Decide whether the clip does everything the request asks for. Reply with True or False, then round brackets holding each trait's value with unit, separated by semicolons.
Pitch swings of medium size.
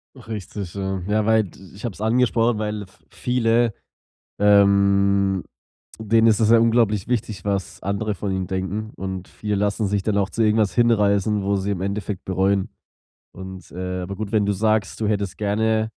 False (2.0 semitones)